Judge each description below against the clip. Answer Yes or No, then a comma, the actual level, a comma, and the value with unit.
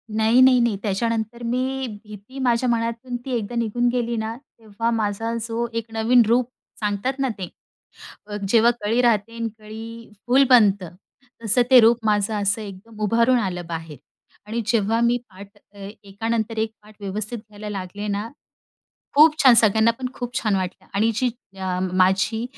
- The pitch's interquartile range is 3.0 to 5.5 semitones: No, narrow, 2.5 semitones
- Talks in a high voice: Yes, high, 225 Hz